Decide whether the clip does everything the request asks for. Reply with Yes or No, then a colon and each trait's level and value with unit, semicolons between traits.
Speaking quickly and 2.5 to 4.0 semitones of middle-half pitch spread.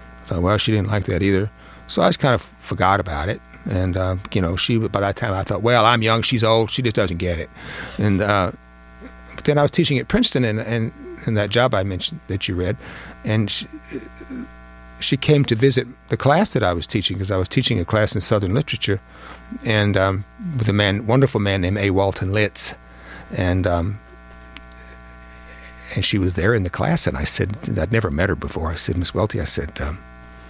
No: fast, 220 wpm; wide, 5.4 semitones